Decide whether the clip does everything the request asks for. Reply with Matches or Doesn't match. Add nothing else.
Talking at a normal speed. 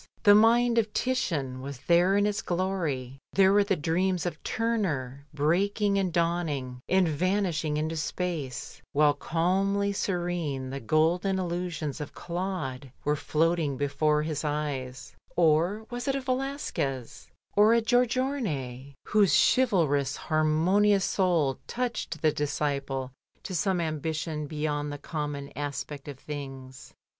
Doesn't match